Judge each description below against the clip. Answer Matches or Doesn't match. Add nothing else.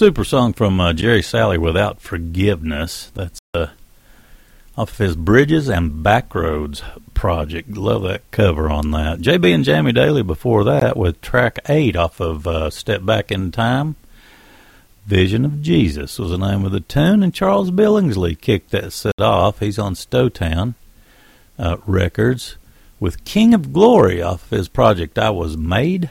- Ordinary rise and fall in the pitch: Doesn't match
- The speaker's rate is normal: Matches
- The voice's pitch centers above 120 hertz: Doesn't match